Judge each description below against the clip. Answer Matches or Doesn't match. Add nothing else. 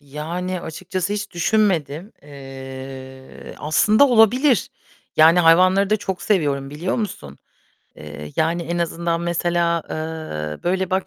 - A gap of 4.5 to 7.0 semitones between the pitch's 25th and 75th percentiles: Matches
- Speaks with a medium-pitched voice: Matches